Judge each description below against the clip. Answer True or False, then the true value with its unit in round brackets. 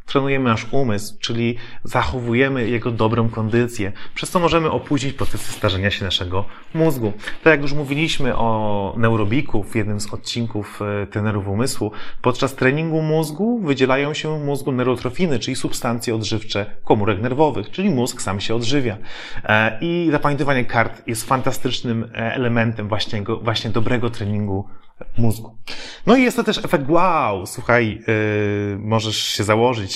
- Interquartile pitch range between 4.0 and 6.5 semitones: True (4.3 semitones)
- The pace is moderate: True (140 wpm)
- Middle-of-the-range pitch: False (115 Hz)